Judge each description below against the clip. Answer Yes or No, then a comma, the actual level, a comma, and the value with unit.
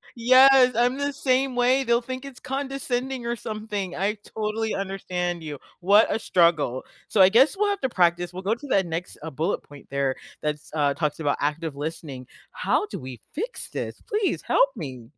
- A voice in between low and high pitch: No, high, 205 Hz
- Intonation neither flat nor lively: No, wide, 8.1 semitones